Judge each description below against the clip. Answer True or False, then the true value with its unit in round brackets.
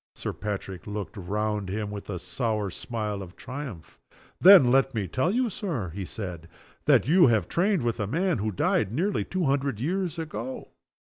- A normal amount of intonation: False (8.3 semitones)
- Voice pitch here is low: True (115 Hz)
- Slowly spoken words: False (170 wpm)